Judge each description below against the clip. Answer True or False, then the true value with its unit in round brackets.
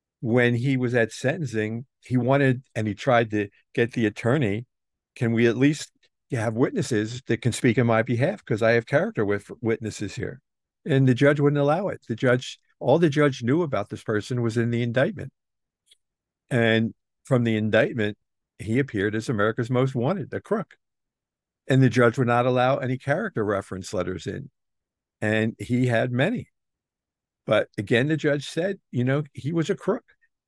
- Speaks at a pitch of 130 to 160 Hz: False (120 Hz)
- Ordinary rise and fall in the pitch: True (3.7 semitones)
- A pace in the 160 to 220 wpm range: True (175 wpm)